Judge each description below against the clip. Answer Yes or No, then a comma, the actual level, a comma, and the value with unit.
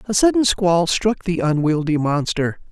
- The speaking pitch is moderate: Yes, medium, 175 Hz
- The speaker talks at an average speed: Yes, average, 155 wpm